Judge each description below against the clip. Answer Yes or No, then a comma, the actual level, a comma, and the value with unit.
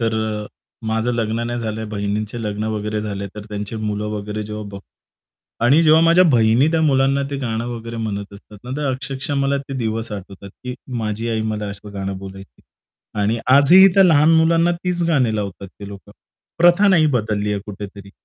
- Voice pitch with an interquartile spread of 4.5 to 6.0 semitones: Yes, average, 4.9 semitones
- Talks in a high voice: No, low, 110 Hz